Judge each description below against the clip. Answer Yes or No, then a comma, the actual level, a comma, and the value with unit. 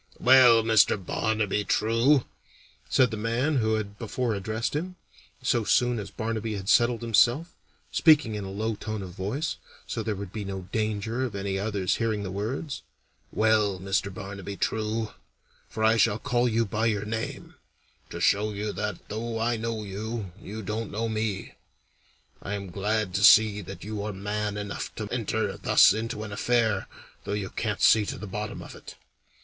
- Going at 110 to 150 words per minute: No, average, 175 wpm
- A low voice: Yes, low, 110 Hz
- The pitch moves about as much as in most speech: No, narrow, 2.1 semitones